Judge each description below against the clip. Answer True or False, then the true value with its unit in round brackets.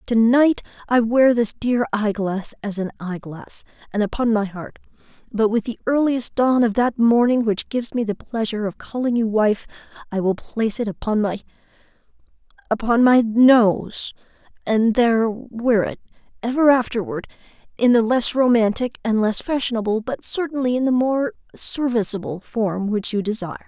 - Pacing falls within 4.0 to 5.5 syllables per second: True (4.9 syllables/s)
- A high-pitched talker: True (225 Hz)